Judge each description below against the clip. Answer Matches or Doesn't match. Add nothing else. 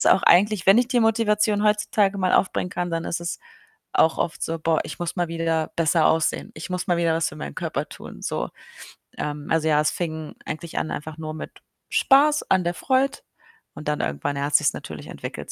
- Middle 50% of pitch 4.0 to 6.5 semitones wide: Matches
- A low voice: Doesn't match